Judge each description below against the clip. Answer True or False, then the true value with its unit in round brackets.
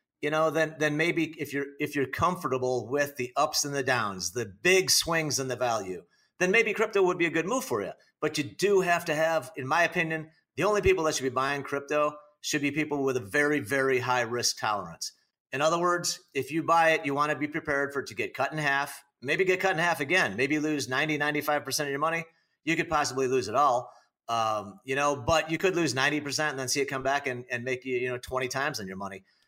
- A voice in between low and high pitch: True (150 Hz)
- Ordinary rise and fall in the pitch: True (3.3 semitones)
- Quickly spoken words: True (245 wpm)